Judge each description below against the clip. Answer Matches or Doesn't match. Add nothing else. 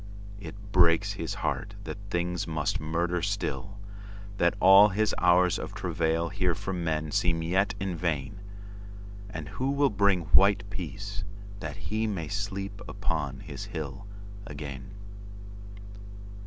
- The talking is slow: Matches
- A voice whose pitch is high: Doesn't match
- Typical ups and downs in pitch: Matches